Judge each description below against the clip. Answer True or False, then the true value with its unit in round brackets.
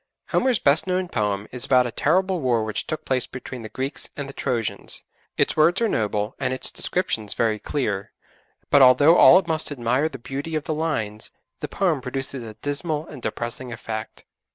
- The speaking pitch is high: False (135 Hz)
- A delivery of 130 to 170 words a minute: False (185 wpm)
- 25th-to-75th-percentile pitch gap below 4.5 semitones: False (5.3 semitones)